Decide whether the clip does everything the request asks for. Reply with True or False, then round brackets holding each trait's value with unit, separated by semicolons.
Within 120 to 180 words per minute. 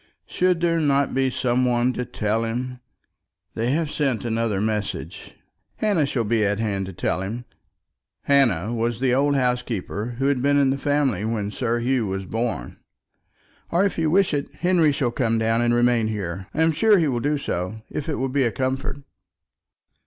False (190 wpm)